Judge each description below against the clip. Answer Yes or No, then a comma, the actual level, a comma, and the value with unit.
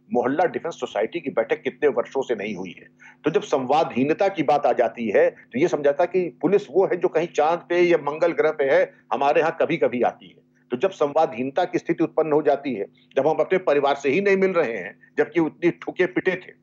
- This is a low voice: No, medium, 170 Hz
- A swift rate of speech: Yes, fast, 235 wpm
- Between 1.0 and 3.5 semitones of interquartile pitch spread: No, average, 3.9 semitones